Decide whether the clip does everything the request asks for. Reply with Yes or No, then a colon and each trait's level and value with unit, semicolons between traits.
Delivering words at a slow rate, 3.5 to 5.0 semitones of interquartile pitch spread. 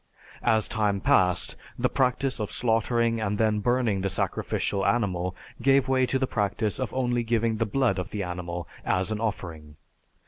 No: average, 170 wpm; average, 4.0 semitones